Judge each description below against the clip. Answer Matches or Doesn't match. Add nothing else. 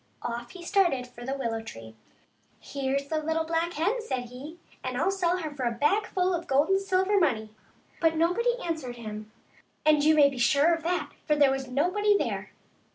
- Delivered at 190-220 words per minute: Matches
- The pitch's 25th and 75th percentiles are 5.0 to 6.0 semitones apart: Matches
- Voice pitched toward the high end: Matches